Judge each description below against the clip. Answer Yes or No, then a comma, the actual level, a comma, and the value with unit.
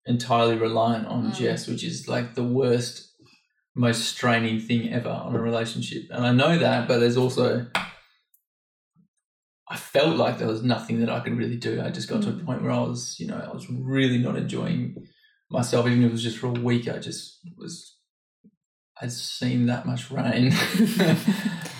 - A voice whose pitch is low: Yes, low, 120 Hz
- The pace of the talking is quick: No, average, 185 wpm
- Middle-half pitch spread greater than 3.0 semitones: No, narrow, 2.5 semitones